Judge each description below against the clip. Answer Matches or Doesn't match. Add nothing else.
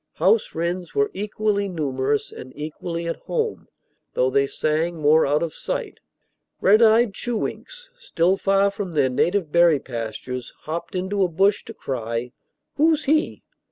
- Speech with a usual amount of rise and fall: Doesn't match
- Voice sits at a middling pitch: Matches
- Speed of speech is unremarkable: Matches